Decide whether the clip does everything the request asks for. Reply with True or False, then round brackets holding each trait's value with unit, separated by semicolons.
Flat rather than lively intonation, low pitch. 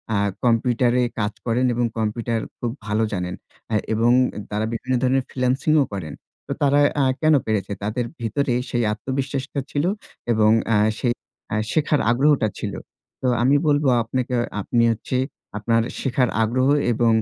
False (3.0 semitones; 120 Hz)